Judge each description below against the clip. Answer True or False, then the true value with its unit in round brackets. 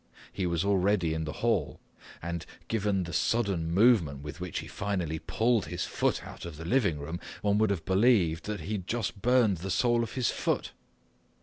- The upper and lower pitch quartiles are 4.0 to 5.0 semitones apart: True (4.7 semitones)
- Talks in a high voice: False (95 Hz)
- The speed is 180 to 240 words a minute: True (195 wpm)